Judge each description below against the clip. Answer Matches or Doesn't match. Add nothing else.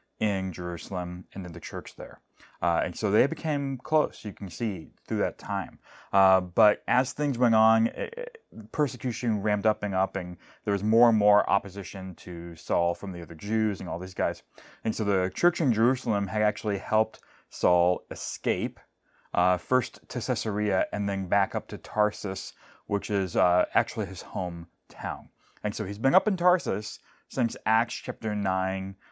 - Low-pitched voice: Matches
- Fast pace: Doesn't match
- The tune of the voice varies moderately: Matches